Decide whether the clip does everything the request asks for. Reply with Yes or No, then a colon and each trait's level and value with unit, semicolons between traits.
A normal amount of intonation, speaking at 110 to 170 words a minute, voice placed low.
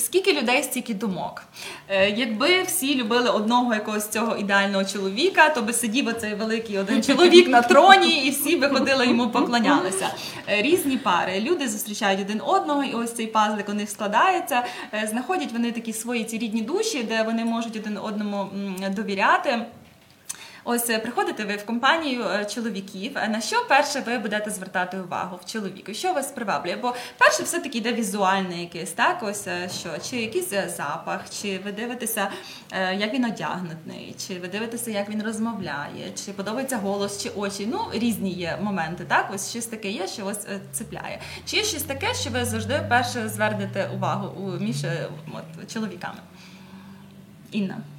No: average, 3.9 semitones; average, 160 wpm; high, 220 Hz